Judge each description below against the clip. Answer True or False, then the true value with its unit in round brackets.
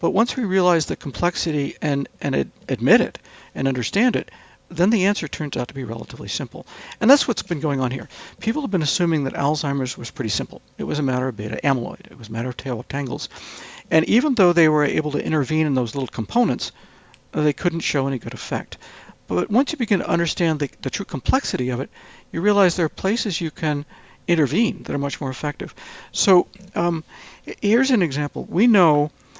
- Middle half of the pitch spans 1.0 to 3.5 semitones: False (5.5 semitones)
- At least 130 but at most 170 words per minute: False (205 wpm)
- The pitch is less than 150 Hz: False (155 Hz)